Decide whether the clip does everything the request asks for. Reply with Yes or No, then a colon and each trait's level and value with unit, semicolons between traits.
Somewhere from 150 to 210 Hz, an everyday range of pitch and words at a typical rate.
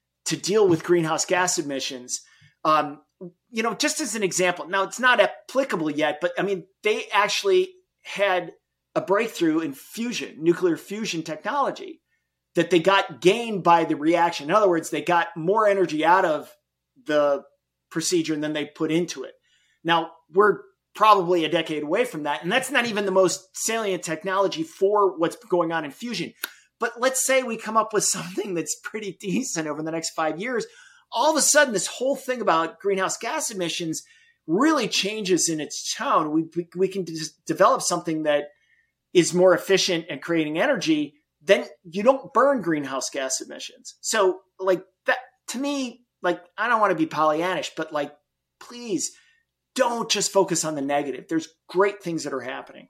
No: medium, 185 Hz; wide, 6.0 semitones; average, 175 wpm